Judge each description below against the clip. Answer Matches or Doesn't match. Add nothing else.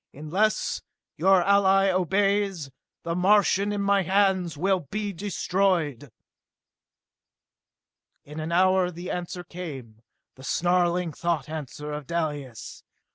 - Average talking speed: Doesn't match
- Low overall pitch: Doesn't match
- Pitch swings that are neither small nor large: Matches